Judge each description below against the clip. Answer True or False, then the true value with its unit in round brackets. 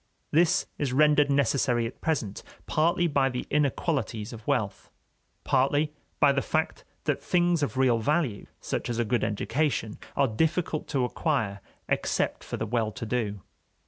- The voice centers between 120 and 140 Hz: True (135 Hz)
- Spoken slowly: False (155 wpm)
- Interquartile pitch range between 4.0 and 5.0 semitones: True (4.6 semitones)